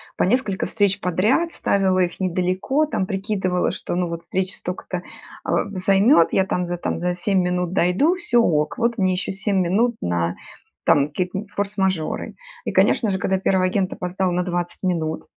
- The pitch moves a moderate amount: No, narrow, 1.9 semitones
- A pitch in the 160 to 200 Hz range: Yes, medium, 185 Hz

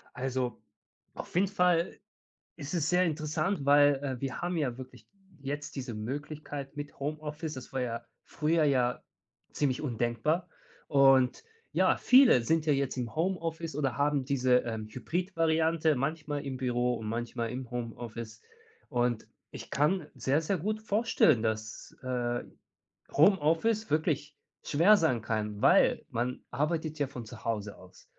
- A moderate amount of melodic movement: Yes, average, 4.6 semitones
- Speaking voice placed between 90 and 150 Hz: Yes, medium, 140 Hz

